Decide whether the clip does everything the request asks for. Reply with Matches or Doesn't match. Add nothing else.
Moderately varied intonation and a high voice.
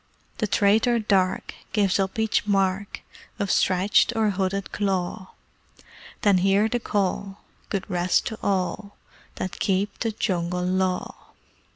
Doesn't match